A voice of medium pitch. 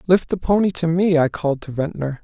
Yes: medium, 165 Hz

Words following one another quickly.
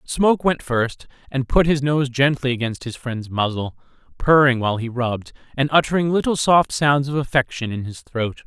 No: average, 185 wpm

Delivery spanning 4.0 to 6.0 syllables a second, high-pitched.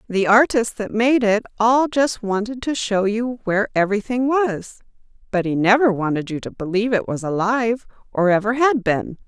Yes: 5.1 syllables/s; high, 220 Hz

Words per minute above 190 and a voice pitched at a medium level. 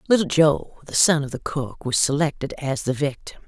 Yes: fast, 205 wpm; medium, 145 Hz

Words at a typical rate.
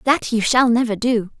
No: fast, 215 wpm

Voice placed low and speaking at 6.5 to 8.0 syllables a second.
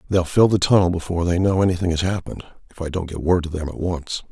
Yes: very low, 90 Hz; 6.6 syllables/s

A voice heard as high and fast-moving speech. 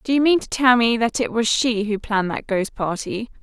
Yes: high, 230 Hz; fast, 265 wpm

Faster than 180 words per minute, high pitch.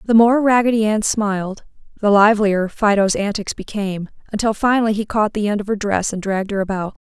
Yes: average, 195 wpm; high, 210 Hz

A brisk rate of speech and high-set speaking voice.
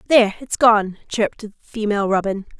No: average, 160 wpm; high, 215 Hz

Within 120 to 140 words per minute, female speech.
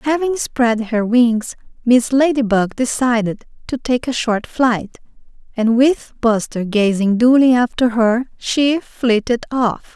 Yes: slow, 135 wpm; female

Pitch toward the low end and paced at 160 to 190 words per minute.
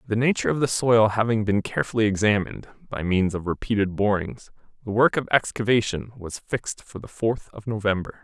Yes: low, 105 Hz; average, 180 wpm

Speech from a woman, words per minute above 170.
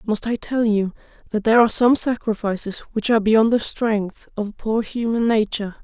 Yes: female; average, 185 wpm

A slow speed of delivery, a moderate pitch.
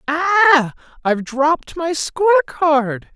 No: slow, 95 wpm; very high, 275 Hz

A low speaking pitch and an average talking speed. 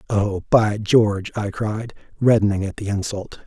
Yes: low, 105 Hz; average, 155 wpm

